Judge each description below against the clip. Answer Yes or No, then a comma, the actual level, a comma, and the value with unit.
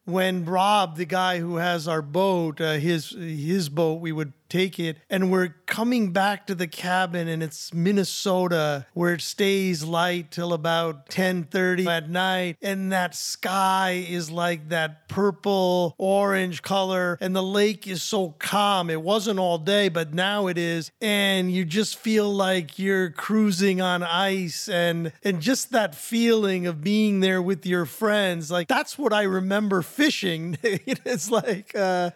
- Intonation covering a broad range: No, narrow, 2.4 semitones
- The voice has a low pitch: No, medium, 185 Hz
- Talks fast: No, average, 165 wpm